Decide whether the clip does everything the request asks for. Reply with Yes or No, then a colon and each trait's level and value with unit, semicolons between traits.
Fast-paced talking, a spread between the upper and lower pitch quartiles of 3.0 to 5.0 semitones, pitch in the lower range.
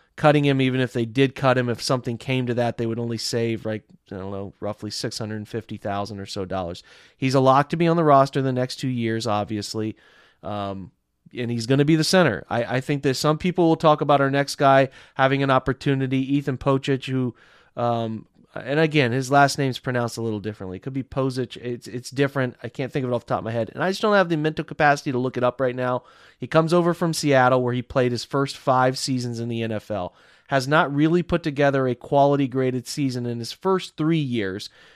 Yes: fast, 235 wpm; average, 3.5 semitones; low, 130 Hz